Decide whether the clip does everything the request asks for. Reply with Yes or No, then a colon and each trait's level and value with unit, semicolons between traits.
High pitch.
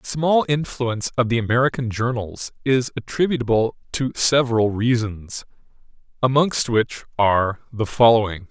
No: low, 120 Hz